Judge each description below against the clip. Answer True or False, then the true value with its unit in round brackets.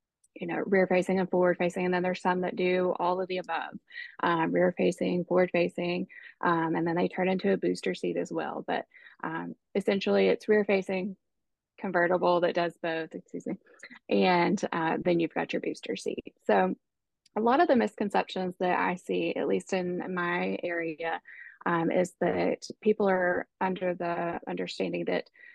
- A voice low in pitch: False (180 Hz)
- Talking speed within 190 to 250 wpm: False (180 wpm)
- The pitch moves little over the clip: True (1.5 semitones)